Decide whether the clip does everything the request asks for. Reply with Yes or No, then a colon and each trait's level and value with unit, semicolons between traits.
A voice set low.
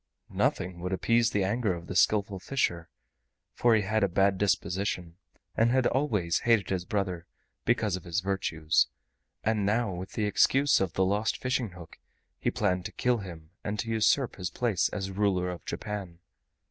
Yes: low, 100 Hz